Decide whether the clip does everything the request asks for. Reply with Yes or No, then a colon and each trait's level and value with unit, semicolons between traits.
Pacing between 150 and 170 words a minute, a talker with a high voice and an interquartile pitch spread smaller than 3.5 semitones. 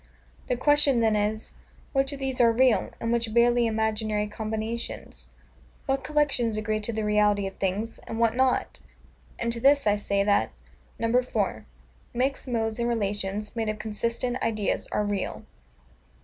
Yes: average, 155 wpm; high, 225 Hz; narrow, 2.5 semitones